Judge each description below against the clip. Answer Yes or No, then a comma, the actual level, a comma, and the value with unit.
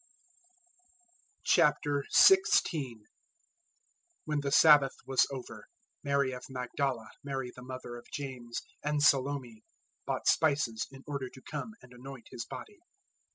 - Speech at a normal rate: No, slow, 115 wpm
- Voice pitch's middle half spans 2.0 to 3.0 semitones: Yes, narrow, 2.6 semitones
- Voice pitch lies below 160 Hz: Yes, low, 135 Hz